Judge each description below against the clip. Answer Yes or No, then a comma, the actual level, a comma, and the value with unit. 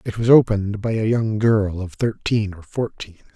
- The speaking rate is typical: Yes, average, 195 wpm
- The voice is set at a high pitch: No, low, 105 Hz